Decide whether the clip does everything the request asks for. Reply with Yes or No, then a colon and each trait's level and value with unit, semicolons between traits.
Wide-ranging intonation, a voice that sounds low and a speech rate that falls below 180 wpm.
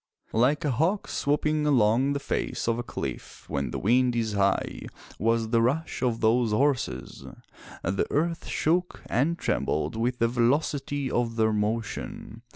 No: average, 4.2 semitones; low, 120 Hz; average, 155 wpm